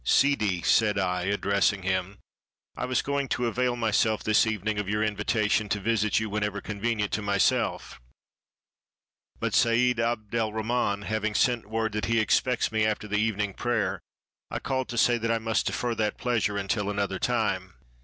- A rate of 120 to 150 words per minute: No, average, 175 wpm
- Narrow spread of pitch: Yes, narrow, 2.2 semitones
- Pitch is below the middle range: Yes, low, 110 Hz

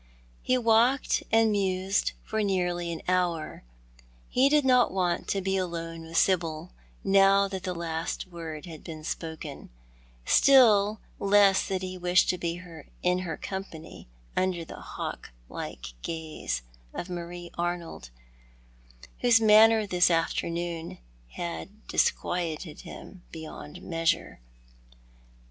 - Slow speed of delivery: Yes, slow, 125 wpm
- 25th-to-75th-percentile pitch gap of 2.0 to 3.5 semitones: Yes, average, 3.0 semitones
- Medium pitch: Yes, medium, 180 Hz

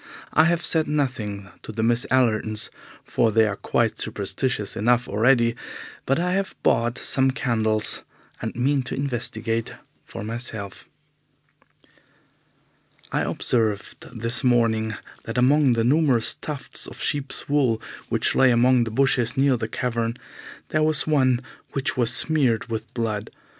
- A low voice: Yes, low, 120 Hz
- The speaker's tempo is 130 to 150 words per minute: Yes, average, 140 wpm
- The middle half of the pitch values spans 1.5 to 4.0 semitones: Yes, average, 3.2 semitones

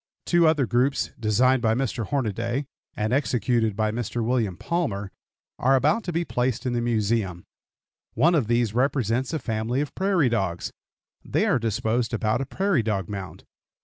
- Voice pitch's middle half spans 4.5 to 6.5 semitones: No, average, 3.8 semitones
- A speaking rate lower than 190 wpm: Yes, average, 165 wpm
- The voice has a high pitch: No, low, 120 Hz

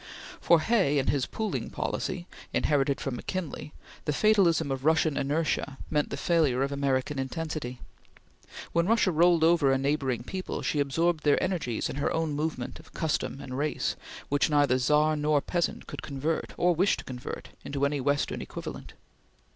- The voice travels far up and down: No, average, 3.2 semitones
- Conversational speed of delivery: Yes, average, 165 wpm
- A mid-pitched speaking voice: Yes, medium, 150 Hz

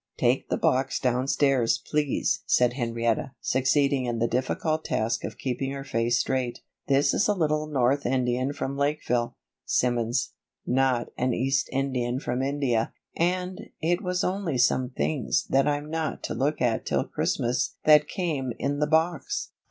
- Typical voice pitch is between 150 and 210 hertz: No, low, 135 Hz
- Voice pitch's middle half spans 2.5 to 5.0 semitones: Yes, average, 3.3 semitones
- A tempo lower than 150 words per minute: No, average, 155 wpm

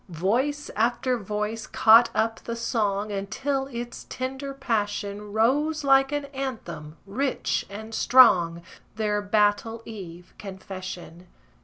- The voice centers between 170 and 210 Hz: No, high, 220 Hz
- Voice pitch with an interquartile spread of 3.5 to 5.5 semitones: Yes, average, 4.4 semitones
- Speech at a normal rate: No, slow, 115 wpm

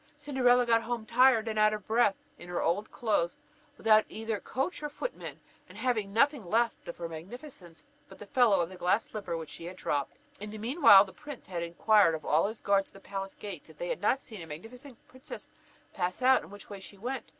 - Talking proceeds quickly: Yes, fast, 230 wpm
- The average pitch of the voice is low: No, high, 215 Hz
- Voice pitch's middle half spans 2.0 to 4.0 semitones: No, average, 5.0 semitones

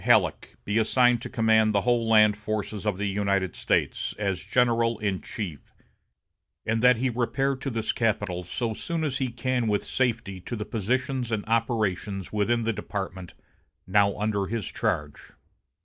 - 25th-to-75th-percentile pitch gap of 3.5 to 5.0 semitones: No, average, 2.9 semitones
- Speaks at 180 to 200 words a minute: No, average, 165 wpm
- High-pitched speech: No, low, 110 Hz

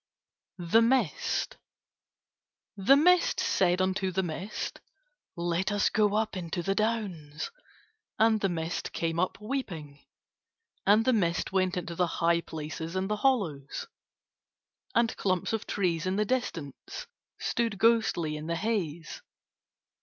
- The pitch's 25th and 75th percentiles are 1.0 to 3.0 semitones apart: No, average, 4.6 semitones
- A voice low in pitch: No, medium, 185 Hz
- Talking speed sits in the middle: No, slow, 130 wpm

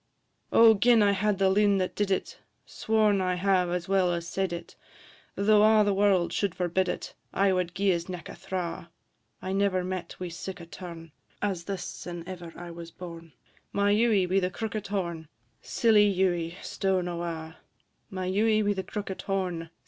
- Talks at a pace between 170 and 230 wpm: Yes, average, 185 wpm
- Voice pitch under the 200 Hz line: Yes, medium, 185 Hz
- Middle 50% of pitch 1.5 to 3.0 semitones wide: Yes, narrow, 2.5 semitones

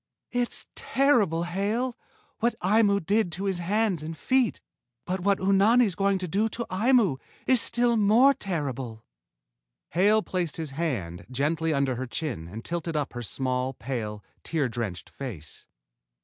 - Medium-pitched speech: Yes, medium, 175 Hz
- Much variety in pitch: Yes, wide, 7.9 semitones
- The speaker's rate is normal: Yes, average, 150 wpm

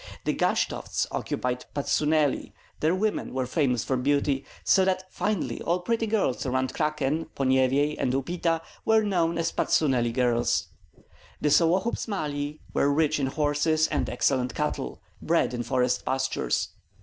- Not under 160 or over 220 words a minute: No, average, 140 wpm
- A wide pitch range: No, average, 4.2 semitones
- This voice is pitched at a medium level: Yes, medium, 145 Hz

